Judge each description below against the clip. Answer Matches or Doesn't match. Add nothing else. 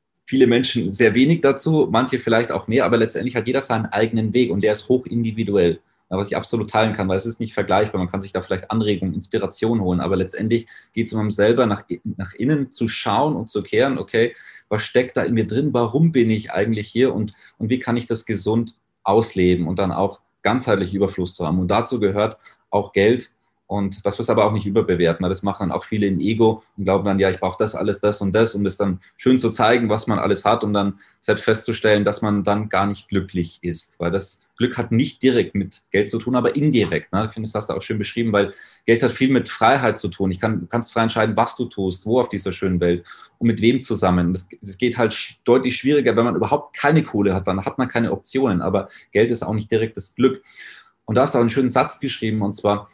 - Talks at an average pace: Doesn't match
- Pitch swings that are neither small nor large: Matches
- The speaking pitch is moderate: Doesn't match